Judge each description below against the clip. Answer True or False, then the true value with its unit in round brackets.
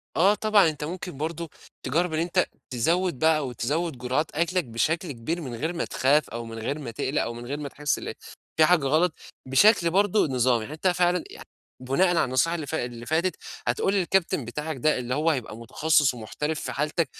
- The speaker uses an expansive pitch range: False (5.0 semitones)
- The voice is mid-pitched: True (155 Hz)